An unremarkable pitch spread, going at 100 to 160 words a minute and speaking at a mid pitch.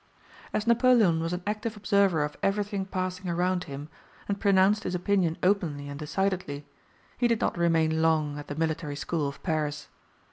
No: average, 4.3 semitones; average, 170 wpm; medium, 180 Hz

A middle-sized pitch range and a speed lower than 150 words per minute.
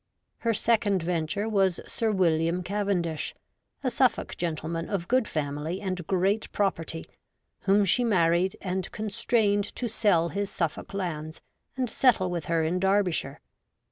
Yes: average, 3.6 semitones; average, 140 wpm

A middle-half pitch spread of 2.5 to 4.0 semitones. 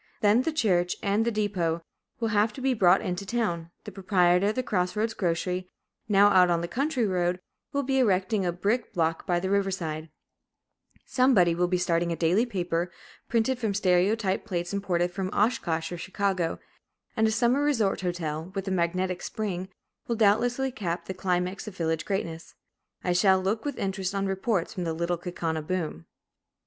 Yes: average, 3.5 semitones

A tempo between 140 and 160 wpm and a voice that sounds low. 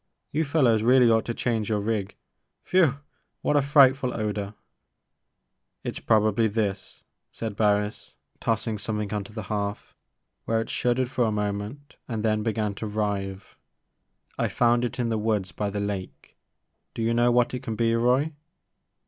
No: average, 170 wpm; low, 110 Hz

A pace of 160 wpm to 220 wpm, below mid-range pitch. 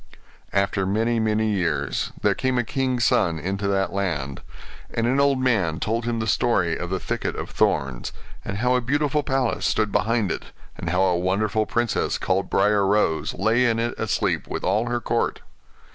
Yes: average, 185 wpm; low, 105 Hz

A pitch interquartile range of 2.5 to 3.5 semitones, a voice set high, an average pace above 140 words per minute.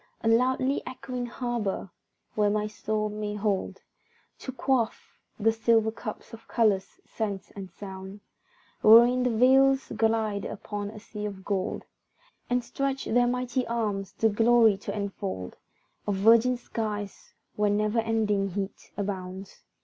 No: average, 2.8 semitones; high, 215 Hz; slow, 135 wpm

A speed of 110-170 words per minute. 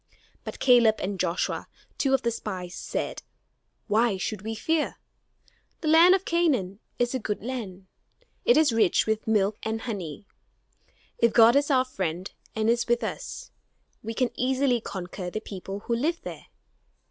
Yes: average, 160 wpm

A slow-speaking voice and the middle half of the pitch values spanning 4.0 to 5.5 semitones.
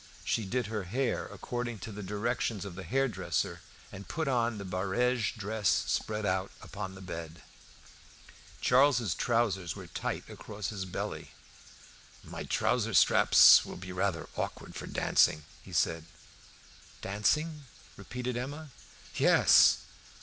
Yes: slow, 130 wpm; average, 4.5 semitones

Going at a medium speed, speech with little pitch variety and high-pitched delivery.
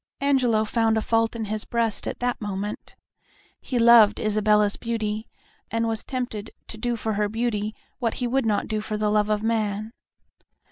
Yes: average, 180 wpm; narrow, 1.6 semitones; high, 220 Hz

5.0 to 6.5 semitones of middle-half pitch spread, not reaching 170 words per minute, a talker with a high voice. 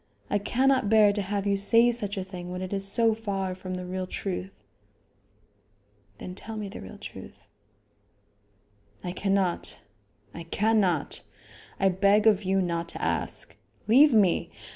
No: narrow, 2.6 semitones; average, 155 wpm; high, 195 Hz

